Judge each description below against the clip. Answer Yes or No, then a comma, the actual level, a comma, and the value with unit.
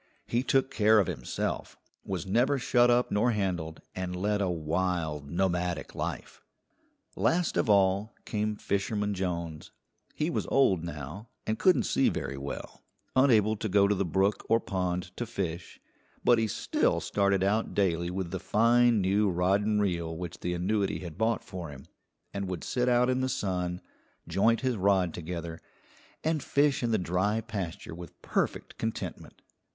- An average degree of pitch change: Yes, average, 4.0 semitones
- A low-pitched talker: Yes, low, 100 Hz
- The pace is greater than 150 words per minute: Yes, average, 165 wpm